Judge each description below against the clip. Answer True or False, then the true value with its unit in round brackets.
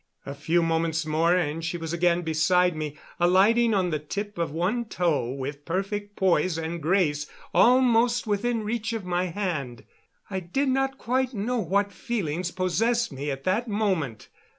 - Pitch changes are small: False (5.0 semitones)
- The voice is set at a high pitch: False (180 Hz)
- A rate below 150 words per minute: False (165 wpm)